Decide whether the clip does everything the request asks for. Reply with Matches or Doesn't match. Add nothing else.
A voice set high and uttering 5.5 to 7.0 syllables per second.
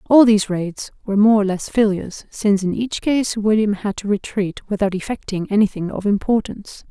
Matches